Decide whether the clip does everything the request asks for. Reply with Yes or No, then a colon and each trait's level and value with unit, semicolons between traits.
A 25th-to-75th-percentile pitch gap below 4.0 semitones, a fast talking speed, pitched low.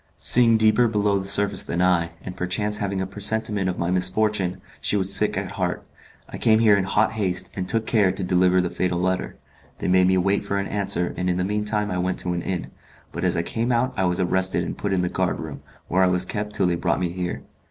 Yes: narrow, 2.4 semitones; fast, 250 wpm; very low, 95 Hz